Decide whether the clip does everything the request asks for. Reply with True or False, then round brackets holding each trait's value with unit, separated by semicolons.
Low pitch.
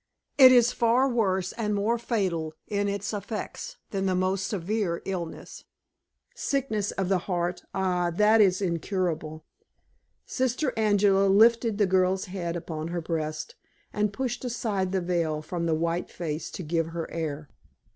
False (190 Hz)